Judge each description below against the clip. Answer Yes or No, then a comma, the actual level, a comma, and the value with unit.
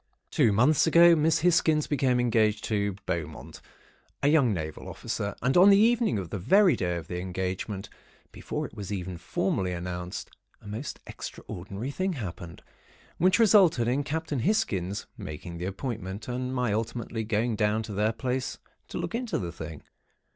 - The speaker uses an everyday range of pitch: No, wide, 7.9 semitones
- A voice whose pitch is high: No, low, 110 Hz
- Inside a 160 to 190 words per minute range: Yes, average, 165 wpm